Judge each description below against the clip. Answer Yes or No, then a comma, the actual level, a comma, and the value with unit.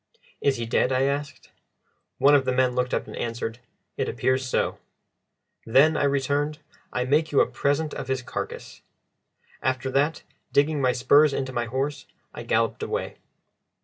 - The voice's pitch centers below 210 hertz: Yes, low, 135 Hz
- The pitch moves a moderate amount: No, narrow, 2.1 semitones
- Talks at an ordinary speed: Yes, average, 165 wpm